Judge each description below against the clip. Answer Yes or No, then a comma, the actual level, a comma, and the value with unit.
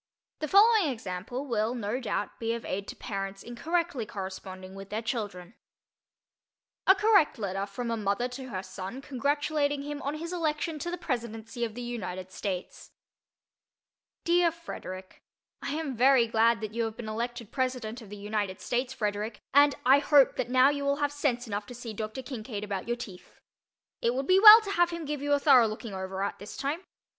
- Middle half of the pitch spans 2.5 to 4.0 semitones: No, wide, 5.6 semitones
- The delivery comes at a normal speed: Yes, average, 195 wpm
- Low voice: No, high, 240 Hz